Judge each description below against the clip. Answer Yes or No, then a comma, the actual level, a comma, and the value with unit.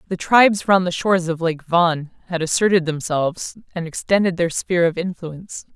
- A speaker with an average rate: Yes, average, 175 wpm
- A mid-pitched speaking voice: Yes, medium, 175 Hz